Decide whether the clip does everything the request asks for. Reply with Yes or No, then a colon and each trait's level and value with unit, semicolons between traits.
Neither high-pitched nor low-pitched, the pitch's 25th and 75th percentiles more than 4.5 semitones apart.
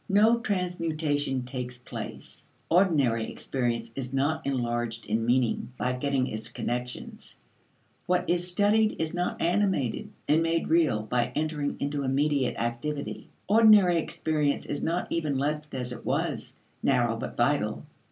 Yes: medium, 145 Hz; average, 5.2 semitones